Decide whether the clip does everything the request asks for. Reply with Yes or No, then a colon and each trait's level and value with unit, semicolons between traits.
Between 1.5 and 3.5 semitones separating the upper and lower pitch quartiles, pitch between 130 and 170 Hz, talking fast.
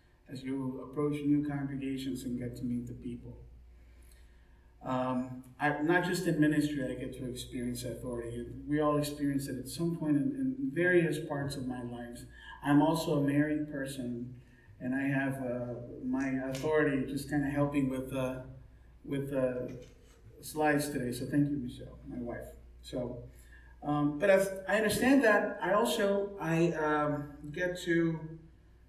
No: average, 3.2 semitones; low, 135 Hz; average, 160 wpm